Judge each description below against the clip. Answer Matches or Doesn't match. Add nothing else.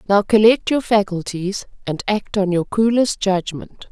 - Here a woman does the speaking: Matches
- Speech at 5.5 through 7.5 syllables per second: Doesn't match